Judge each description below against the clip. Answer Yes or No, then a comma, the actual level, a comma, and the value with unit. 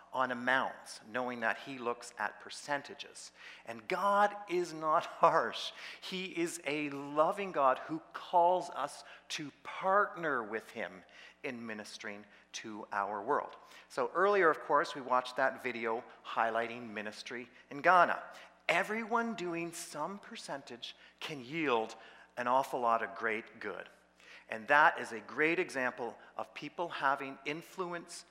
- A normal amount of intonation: No, wide, 6.8 semitones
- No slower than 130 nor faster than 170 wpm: Yes, slow, 135 wpm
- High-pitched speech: No, low, 135 Hz